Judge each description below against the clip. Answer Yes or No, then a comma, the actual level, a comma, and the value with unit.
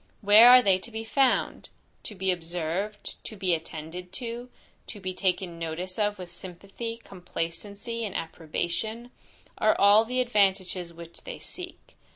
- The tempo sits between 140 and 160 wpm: Yes, average, 150 wpm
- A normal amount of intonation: Yes, average, 4.3 semitones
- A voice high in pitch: Yes, high, 195 Hz